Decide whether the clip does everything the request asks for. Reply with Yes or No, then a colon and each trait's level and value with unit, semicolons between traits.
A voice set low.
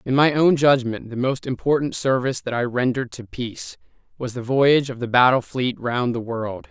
Yes: low, 125 Hz